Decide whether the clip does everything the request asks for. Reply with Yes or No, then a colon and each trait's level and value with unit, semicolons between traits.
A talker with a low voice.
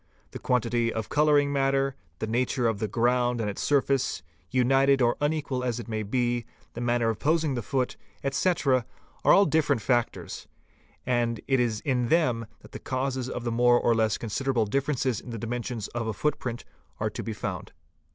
Yes: low, 125 Hz